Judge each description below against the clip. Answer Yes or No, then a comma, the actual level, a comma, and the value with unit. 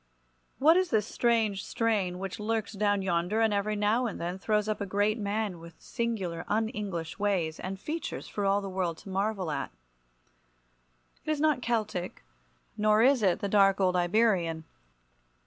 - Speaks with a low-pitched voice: No, high, 205 Hz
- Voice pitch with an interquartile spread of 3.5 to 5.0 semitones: No, average, 3.0 semitones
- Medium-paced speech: Yes, average, 170 wpm